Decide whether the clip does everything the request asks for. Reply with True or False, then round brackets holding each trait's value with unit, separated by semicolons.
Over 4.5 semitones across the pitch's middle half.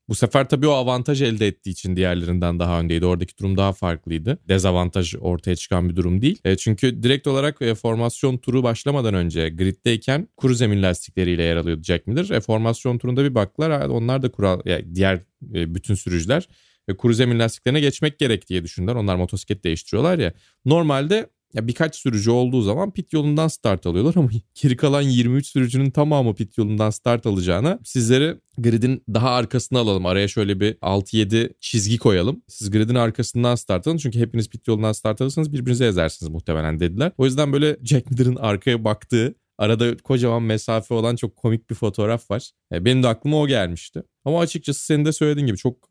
True (5.2 semitones)